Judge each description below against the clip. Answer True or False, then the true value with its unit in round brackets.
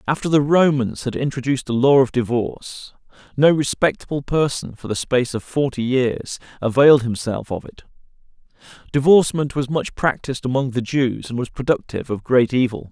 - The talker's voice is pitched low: True (130 Hz)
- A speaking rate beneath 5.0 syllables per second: False (5.5 syllables/s)